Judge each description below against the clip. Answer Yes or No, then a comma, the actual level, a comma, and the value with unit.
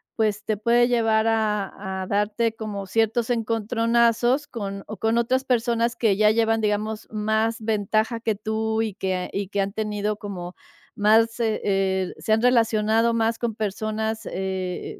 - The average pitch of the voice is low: No, high, 220 Hz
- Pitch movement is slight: Yes, narrow, 1.8 semitones